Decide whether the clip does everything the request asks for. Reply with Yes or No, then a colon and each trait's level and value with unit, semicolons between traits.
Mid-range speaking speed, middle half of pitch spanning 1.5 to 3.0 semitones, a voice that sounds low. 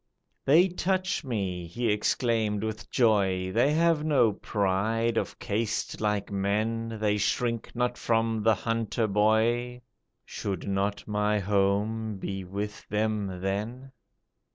No: slow, 125 wpm; narrow, 2.6 semitones; low, 110 Hz